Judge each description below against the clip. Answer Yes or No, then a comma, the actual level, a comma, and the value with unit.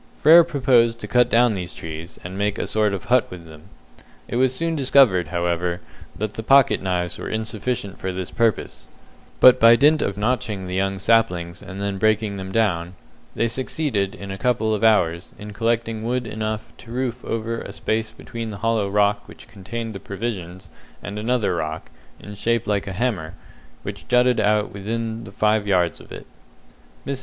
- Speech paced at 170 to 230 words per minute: Yes, average, 185 wpm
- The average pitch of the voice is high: No, low, 110 Hz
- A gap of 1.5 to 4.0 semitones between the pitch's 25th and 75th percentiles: Yes, average, 3.4 semitones